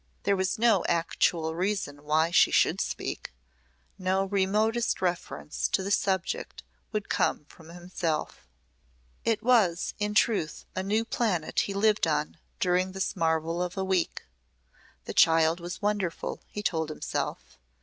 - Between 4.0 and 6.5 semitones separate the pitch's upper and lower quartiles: No, average, 3.6 semitones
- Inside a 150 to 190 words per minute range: No, average, 140 wpm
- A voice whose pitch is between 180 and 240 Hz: Yes, medium, 185 Hz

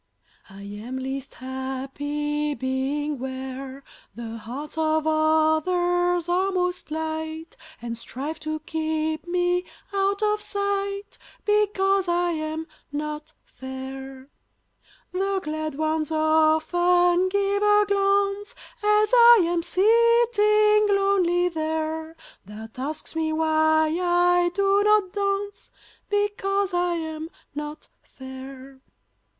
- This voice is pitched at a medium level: No, very high, 320 Hz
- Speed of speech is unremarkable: No, slow, 105 wpm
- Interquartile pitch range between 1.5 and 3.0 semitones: No, average, 4.8 semitones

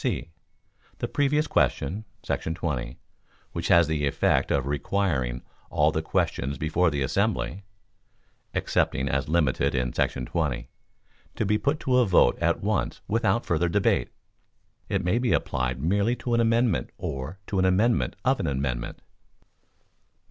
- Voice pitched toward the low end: Yes, very low, 80 Hz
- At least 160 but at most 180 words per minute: No, average, 145 wpm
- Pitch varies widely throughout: Yes, wide, 7.8 semitones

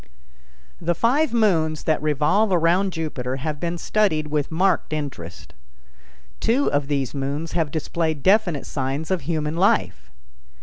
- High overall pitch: No, medium, 160 Hz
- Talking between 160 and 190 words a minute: No, slow, 135 wpm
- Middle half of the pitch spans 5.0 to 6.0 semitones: No, average, 4.1 semitones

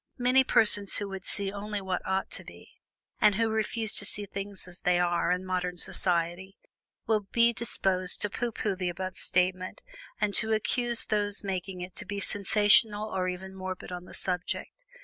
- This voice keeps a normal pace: Yes, average, 185 wpm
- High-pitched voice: Yes, high, 195 Hz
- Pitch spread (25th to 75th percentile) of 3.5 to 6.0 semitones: No, narrow, 2.4 semitones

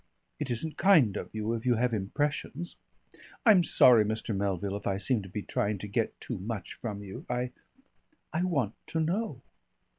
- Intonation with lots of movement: Yes, wide, 6.2 semitones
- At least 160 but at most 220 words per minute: Yes, average, 180 wpm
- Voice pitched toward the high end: No, low, 115 Hz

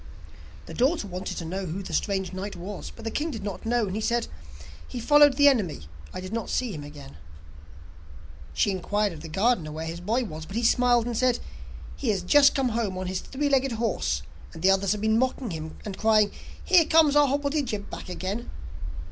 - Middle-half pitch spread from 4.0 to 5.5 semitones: Yes, average, 5.2 semitones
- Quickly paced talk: Yes, fast, 215 wpm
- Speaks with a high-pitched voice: Yes, high, 215 Hz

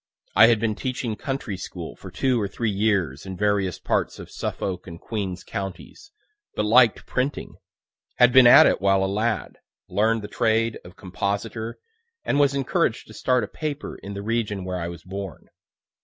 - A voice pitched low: Yes, low, 105 Hz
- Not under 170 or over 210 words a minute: Yes, average, 180 wpm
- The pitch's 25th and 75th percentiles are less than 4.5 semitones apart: Yes, average, 3.6 semitones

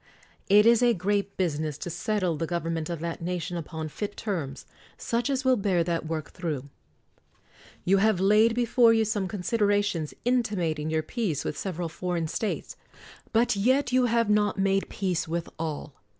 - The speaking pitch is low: No, high, 190 Hz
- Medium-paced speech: Yes, average, 175 wpm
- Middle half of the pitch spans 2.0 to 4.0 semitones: No, average, 4.8 semitones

